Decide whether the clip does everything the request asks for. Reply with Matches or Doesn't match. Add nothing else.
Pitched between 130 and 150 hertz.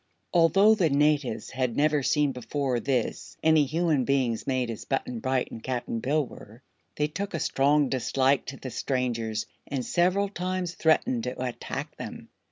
Matches